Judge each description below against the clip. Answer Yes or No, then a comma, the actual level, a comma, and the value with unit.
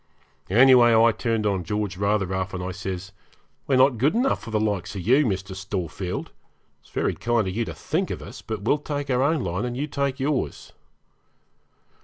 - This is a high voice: No, low, 110 Hz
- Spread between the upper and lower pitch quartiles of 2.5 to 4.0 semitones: No, wide, 5.6 semitones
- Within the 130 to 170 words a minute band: No, average, 200 wpm